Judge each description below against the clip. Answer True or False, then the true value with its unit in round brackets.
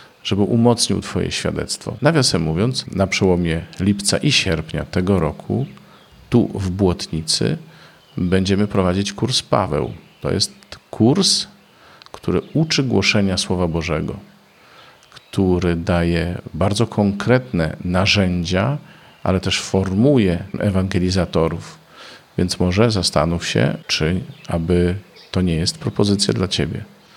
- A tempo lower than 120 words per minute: True (110 wpm)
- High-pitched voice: False (95 Hz)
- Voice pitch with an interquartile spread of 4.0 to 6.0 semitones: True (4.6 semitones)